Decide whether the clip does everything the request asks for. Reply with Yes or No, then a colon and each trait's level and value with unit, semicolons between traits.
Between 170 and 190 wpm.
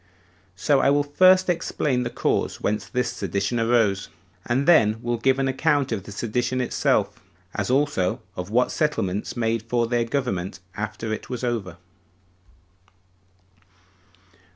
No: average, 140 wpm